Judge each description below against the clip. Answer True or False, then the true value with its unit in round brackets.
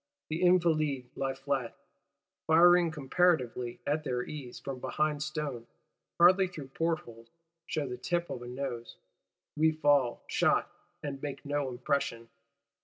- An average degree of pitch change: True (4.0 semitones)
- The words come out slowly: True (130 wpm)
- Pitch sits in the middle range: True (145 Hz)